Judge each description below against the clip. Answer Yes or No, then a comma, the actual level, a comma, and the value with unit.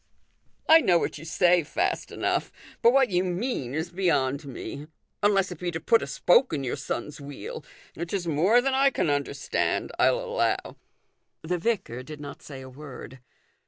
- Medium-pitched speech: Yes, medium, 170 Hz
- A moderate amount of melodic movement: No, wide, 6.0 semitones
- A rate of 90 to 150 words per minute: No, average, 185 wpm